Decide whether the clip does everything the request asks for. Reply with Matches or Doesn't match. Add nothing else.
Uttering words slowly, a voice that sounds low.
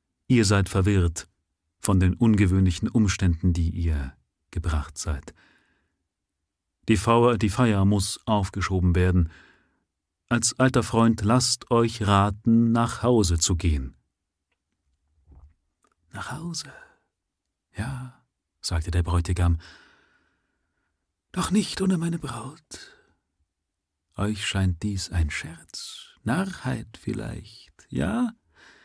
Matches